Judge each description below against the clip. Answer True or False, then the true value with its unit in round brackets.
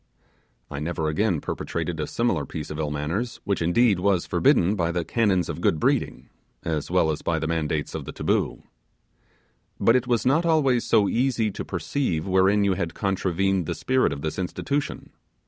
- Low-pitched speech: True (95 Hz)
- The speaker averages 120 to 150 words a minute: False (180 wpm)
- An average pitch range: False (6.2 semitones)